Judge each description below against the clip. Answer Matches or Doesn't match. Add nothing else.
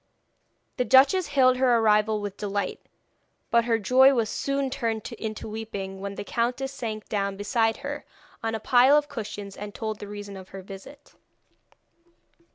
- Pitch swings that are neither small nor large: Matches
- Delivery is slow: Doesn't match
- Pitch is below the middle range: Doesn't match